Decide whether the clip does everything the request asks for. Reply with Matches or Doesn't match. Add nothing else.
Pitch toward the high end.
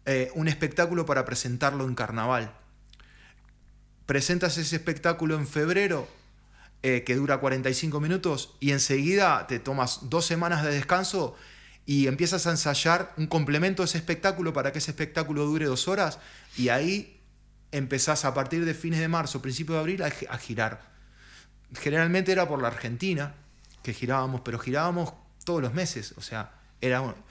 Doesn't match